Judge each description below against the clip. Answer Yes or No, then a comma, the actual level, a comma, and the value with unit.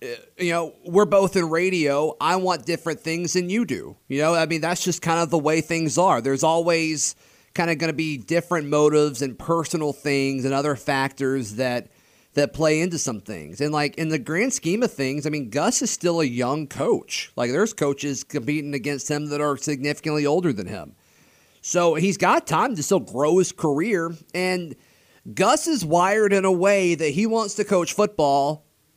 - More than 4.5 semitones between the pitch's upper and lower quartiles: No, average, 3.5 semitones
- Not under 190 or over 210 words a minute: Yes, average, 200 wpm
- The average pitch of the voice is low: No, medium, 160 Hz